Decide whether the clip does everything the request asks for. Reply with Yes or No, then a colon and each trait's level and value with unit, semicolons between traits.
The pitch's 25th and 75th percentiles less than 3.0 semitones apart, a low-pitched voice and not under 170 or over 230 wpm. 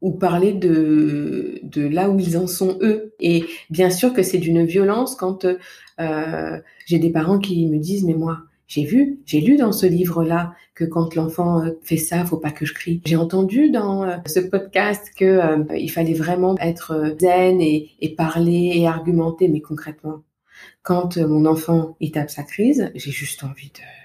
No: narrow, 2.6 semitones; medium, 170 Hz; average, 185 wpm